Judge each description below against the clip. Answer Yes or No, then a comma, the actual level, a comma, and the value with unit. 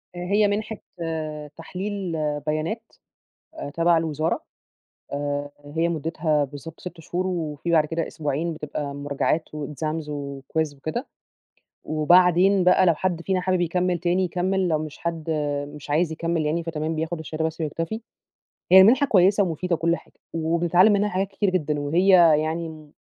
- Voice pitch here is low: No, medium, 165 Hz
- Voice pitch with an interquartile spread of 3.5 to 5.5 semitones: No, average, 3.0 semitones